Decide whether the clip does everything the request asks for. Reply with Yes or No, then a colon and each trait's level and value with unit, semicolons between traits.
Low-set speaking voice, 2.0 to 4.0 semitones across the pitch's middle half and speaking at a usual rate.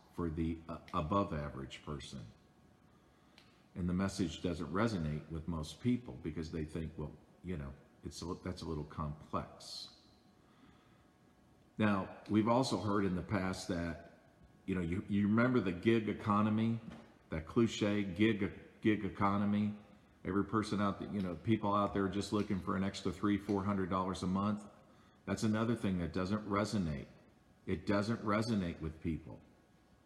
Yes: low, 100 Hz; average, 3.7 semitones; average, 160 wpm